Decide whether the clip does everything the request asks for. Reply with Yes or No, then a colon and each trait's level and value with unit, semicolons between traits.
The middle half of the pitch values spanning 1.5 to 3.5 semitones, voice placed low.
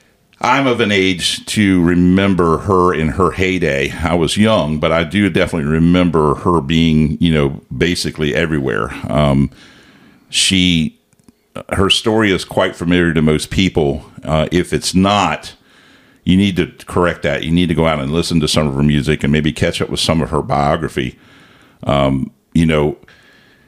Yes: average, 3.0 semitones; very low, 80 Hz